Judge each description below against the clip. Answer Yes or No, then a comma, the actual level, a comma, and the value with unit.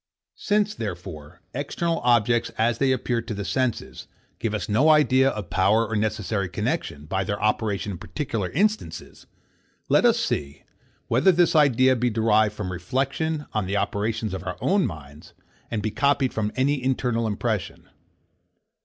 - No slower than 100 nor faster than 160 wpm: Yes, average, 155 wpm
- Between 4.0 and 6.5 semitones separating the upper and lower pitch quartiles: Yes, average, 4.8 semitones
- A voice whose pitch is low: Yes, low, 115 Hz